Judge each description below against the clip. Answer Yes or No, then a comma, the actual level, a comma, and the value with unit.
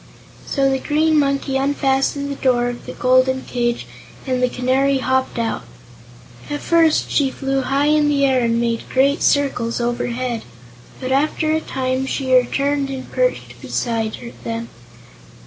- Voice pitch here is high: Yes, very high, 265 Hz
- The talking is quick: No, average, 150 wpm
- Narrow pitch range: Yes, narrow, 2.1 semitones